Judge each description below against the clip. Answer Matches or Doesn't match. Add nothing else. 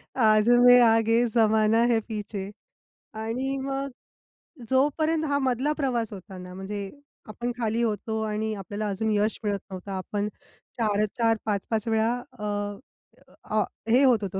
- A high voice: Matches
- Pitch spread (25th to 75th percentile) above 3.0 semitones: Doesn't match